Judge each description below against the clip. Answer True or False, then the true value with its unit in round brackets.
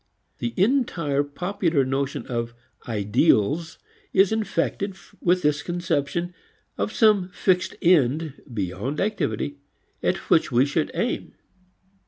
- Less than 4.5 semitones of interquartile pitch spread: False (5.2 semitones)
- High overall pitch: False (160 Hz)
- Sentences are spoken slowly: True (110 wpm)